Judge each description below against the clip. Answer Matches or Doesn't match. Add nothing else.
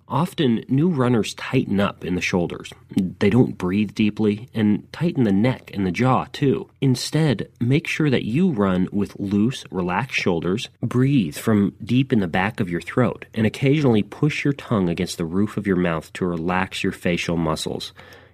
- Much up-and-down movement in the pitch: Matches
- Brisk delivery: Doesn't match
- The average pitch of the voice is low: Matches